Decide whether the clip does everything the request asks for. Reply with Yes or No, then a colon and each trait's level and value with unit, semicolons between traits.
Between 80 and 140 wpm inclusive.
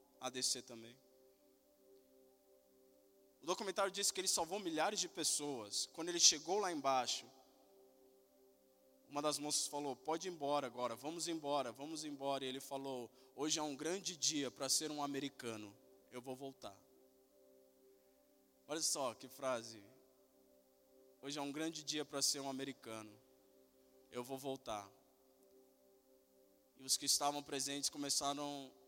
Yes: average, 135 wpm